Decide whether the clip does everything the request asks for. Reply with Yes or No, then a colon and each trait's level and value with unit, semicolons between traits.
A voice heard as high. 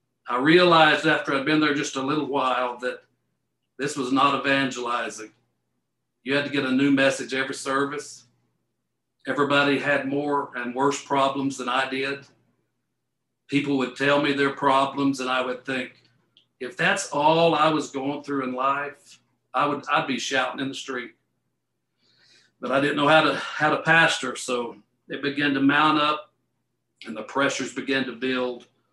No: low, 135 Hz